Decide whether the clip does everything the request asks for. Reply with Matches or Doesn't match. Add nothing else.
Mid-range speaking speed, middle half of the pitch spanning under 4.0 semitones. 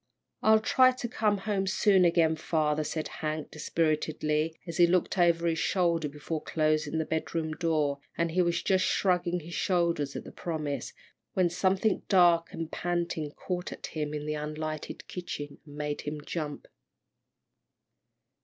Matches